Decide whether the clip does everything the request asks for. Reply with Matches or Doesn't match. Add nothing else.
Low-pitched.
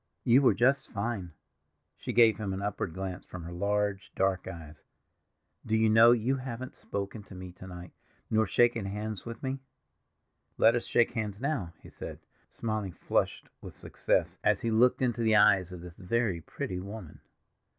Matches